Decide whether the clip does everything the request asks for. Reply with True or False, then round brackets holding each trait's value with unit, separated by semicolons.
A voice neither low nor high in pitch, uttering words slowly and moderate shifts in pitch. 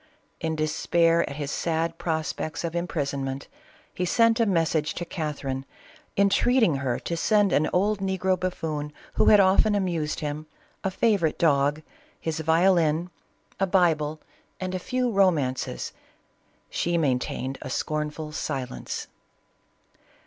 True (165 Hz; 130 wpm; 3.7 semitones)